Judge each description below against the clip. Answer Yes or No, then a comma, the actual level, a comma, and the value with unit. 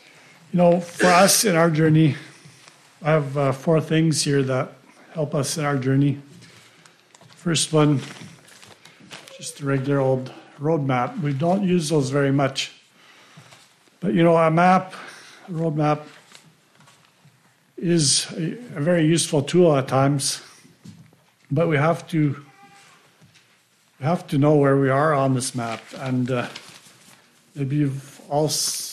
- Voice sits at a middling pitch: Yes, medium, 150 Hz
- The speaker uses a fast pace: No, slow, 135 wpm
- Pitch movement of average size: Yes, average, 3.2 semitones